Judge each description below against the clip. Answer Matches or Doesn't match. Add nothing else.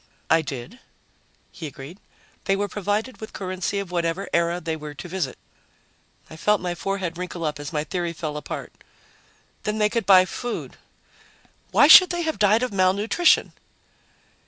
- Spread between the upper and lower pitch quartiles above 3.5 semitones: Matches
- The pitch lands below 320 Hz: Matches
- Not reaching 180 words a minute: Matches